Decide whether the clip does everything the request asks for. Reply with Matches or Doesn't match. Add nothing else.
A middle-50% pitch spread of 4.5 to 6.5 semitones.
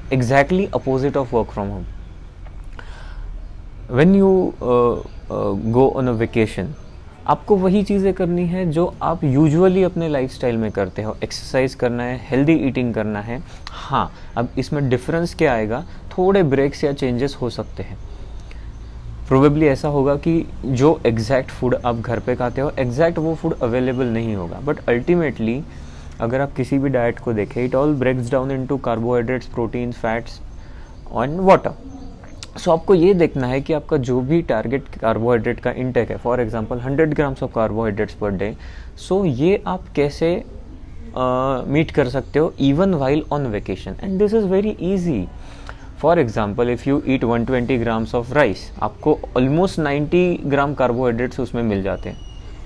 Matches